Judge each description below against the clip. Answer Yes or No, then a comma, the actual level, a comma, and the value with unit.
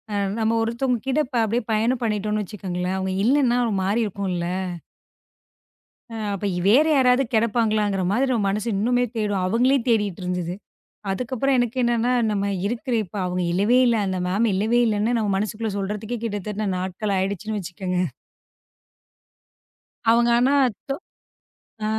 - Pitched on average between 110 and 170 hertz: No, high, 215 Hz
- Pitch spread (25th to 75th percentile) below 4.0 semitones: Yes, average, 3.4 semitones